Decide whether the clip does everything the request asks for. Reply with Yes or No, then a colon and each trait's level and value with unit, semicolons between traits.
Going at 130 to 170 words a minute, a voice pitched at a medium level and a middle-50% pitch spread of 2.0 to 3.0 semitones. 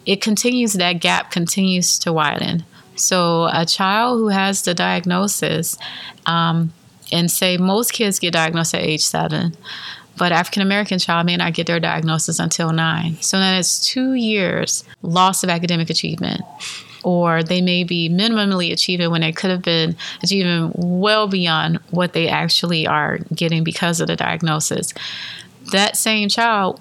Yes: average, 155 wpm; medium, 175 Hz; narrow, 2.5 semitones